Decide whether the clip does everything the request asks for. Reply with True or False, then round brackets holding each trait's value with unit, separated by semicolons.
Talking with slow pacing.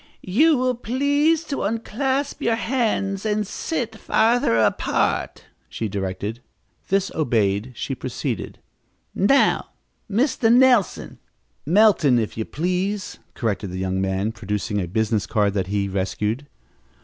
True (130 wpm)